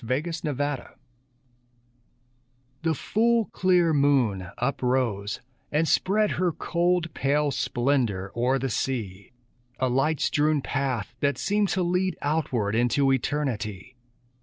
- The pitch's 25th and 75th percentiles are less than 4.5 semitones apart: No, average, 4.9 semitones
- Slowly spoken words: Yes, slow, 115 wpm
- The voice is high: No, medium, 140 Hz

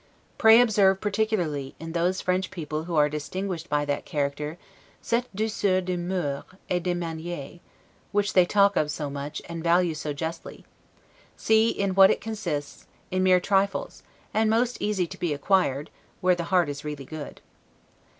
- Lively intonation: No, average, 4.5 semitones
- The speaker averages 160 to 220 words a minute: Yes, average, 165 wpm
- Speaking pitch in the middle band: Yes, medium, 175 Hz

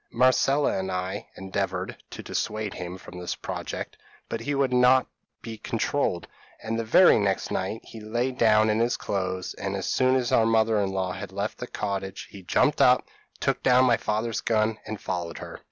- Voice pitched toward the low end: Yes, low, 110 Hz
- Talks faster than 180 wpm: Yes, average, 190 wpm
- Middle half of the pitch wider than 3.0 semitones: Yes, average, 3.6 semitones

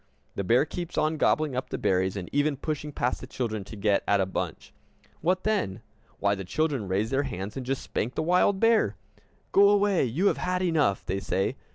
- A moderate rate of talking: No, fast, 210 wpm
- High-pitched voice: No, low, 135 Hz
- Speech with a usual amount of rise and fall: No, wide, 8.7 semitones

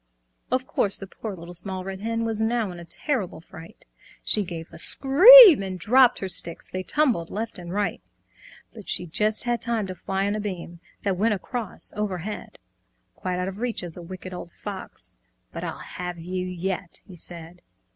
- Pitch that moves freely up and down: No, average, 3.9 semitones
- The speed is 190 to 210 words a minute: Yes, average, 195 wpm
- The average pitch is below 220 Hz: Yes, high, 190 Hz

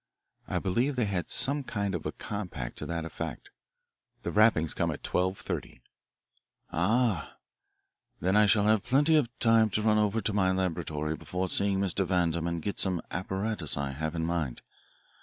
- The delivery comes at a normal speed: Yes, average, 175 wpm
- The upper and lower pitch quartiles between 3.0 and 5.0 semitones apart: Yes, average, 4.1 semitones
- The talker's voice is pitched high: No, very low, 95 Hz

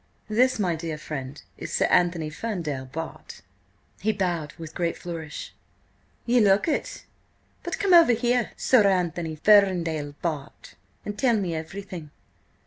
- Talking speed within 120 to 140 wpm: Yes, slow, 135 wpm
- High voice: No, medium, 175 Hz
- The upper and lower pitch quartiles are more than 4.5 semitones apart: Yes, average, 5.1 semitones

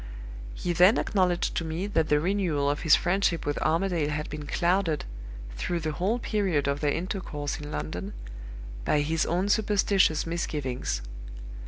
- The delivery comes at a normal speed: Yes, average, 155 wpm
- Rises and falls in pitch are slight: No, average, 4.1 semitones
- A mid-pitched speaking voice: Yes, medium, 165 Hz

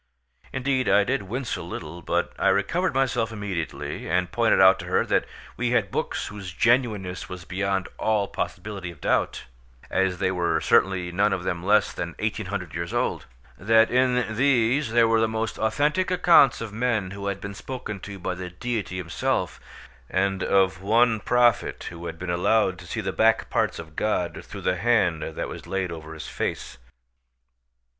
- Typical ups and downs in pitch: Yes, average, 3.9 semitones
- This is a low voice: Yes, low, 100 Hz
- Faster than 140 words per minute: Yes, average, 180 wpm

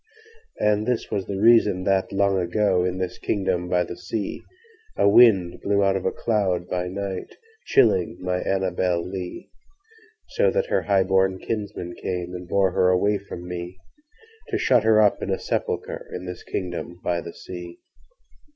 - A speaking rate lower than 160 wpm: Yes, average, 145 wpm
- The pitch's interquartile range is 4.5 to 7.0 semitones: No, average, 3.1 semitones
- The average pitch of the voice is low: Yes, very low, 95 Hz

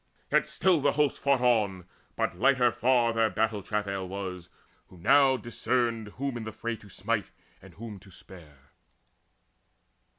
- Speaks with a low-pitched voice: Yes, low, 110 Hz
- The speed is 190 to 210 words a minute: No, average, 155 wpm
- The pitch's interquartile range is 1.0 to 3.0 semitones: No, average, 4.5 semitones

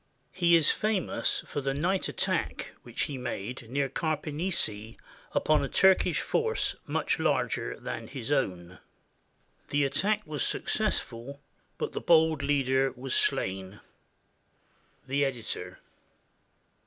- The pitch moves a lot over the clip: No, average, 4.4 semitones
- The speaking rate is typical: No, slow, 115 wpm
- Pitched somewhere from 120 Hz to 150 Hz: Yes, medium, 140 Hz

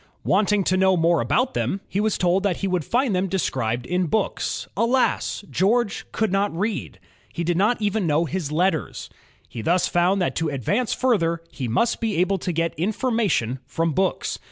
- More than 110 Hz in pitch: Yes, medium, 185 Hz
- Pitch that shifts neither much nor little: Yes, average, 3.9 semitones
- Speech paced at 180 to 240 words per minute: Yes, average, 190 wpm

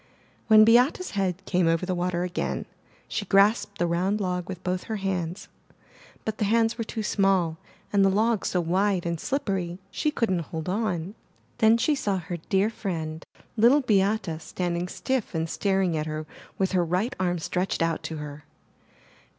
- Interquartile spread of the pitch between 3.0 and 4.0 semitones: Yes, average, 3.6 semitones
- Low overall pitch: No, high, 190 Hz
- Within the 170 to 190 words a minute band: Yes, average, 175 wpm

